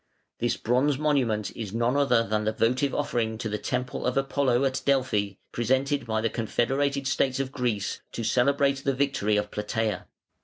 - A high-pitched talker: No, low, 125 Hz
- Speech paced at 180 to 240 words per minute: No, average, 170 wpm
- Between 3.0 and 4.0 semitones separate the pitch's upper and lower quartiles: Yes, average, 3.6 semitones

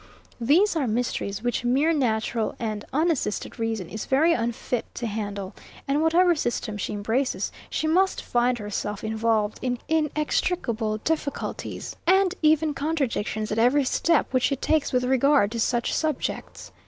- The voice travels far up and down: Yes, wide, 5.7 semitones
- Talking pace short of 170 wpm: Yes, average, 145 wpm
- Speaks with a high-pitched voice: Yes, very high, 250 Hz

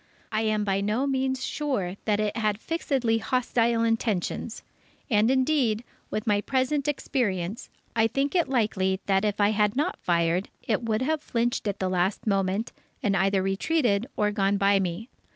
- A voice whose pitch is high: Yes, high, 215 Hz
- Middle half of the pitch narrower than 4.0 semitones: No, average, 4.3 semitones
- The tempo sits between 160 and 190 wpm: Yes, average, 170 wpm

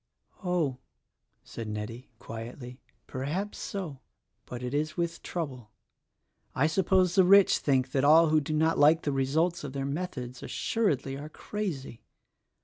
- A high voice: No, medium, 145 Hz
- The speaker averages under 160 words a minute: Yes, average, 140 wpm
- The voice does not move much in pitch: No, average, 4.8 semitones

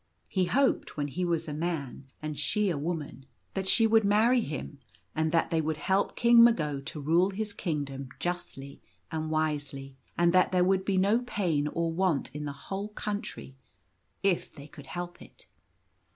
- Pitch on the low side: No, medium, 170 Hz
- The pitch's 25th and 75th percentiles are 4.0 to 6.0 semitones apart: Yes, average, 4.6 semitones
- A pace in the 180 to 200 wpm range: Yes, average, 195 wpm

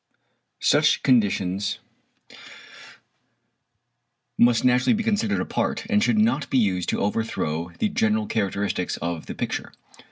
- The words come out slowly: Yes, slow, 120 wpm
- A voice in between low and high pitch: No, low, 120 Hz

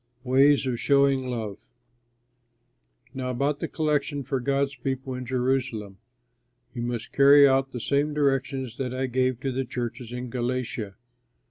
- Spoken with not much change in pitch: Yes, narrow, 2.0 semitones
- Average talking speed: Yes, average, 145 wpm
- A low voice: Yes, low, 130 Hz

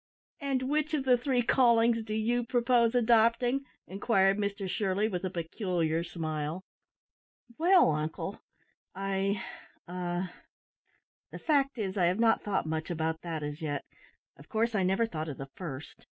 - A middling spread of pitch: No, wide, 5.7 semitones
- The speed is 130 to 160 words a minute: Yes, average, 155 wpm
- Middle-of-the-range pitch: No, high, 195 Hz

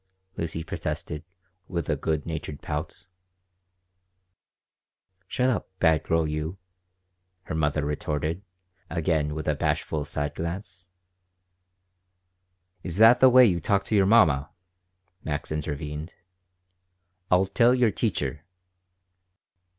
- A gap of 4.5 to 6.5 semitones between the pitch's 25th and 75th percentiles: No, average, 4.0 semitones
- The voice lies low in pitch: Yes, very low, 80 Hz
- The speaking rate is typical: No, slow, 110 wpm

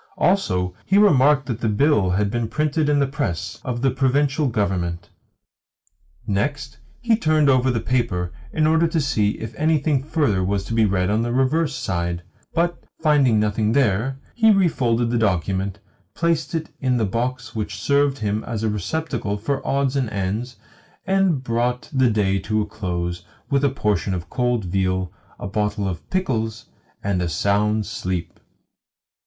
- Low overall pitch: Yes, low, 115 Hz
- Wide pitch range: Yes, wide, 5.8 semitones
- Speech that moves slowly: No, average, 165 wpm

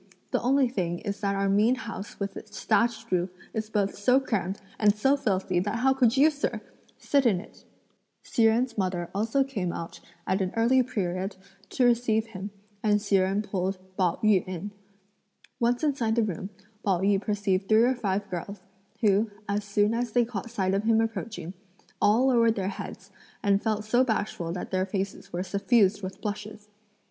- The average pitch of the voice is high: Yes, high, 210 Hz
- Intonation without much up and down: No, average, 3.2 semitones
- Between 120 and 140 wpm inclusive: No, average, 185 wpm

